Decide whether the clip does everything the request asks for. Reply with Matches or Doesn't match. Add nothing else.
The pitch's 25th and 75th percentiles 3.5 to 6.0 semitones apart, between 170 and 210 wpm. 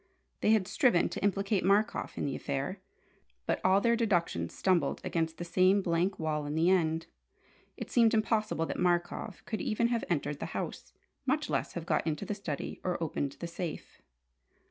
Matches